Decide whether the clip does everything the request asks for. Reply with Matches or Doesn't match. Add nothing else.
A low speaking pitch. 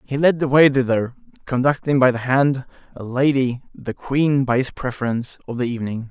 Matches